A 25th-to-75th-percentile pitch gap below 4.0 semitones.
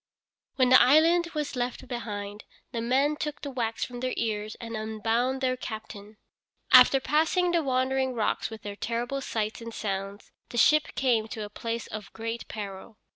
Yes: average, 3.3 semitones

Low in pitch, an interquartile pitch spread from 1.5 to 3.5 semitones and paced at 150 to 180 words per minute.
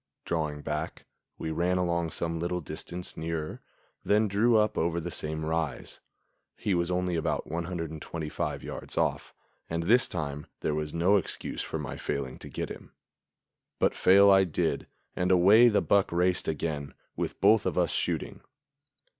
Yes: very low, 85 Hz; average, 2.8 semitones; average, 160 wpm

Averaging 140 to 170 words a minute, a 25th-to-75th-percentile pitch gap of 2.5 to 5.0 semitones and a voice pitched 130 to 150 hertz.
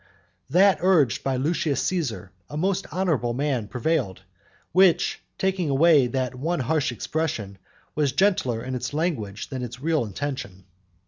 No: average, 145 wpm; wide, 5.4 semitones; medium, 140 Hz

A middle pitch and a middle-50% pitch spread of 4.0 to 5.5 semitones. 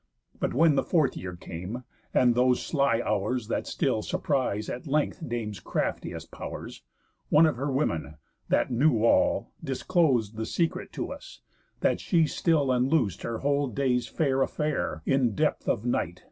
No: low, 125 Hz; average, 4.6 semitones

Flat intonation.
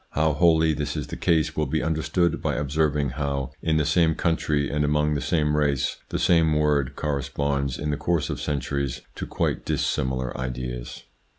Yes: narrow, 2.0 semitones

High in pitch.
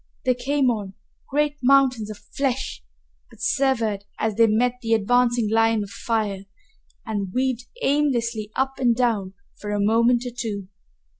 Yes: high, 230 Hz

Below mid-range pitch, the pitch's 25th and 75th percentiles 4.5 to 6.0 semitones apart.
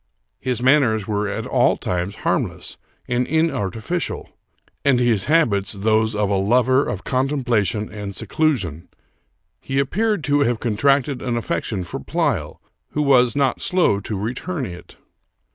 Yes: low, 120 Hz; average, 5.2 semitones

